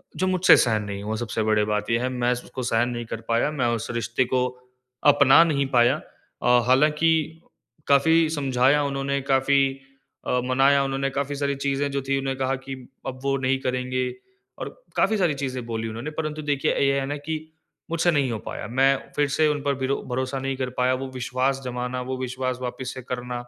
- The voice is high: No, low, 135 Hz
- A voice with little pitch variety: Yes, narrow, 2.2 semitones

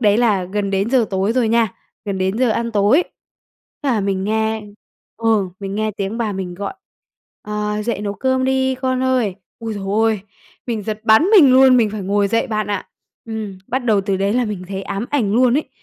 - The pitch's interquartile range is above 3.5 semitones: No, average, 3.2 semitones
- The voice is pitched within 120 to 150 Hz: No, high, 215 Hz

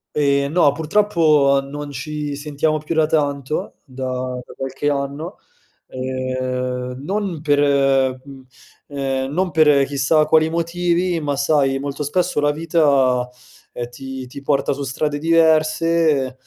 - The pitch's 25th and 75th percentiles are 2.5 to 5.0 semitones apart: Yes, average, 2.8 semitones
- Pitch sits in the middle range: Yes, medium, 145 Hz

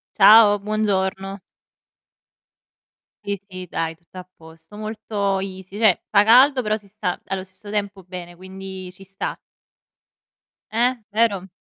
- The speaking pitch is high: Yes, high, 195 Hz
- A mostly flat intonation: Yes, narrow, 2.2 semitones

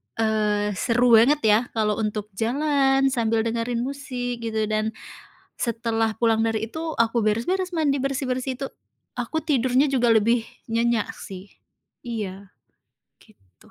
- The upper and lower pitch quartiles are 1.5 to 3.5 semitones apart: Yes, average, 3.2 semitones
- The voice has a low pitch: No, high, 230 Hz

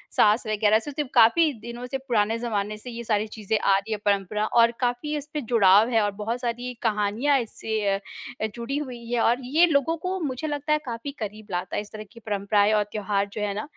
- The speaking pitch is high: Yes, high, 230 Hz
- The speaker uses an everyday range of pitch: Yes, average, 3.2 semitones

